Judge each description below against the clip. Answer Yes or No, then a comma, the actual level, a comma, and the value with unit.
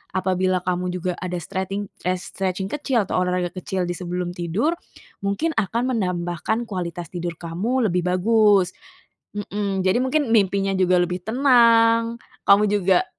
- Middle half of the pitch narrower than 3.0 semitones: No, average, 3.5 semitones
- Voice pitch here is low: No, high, 190 Hz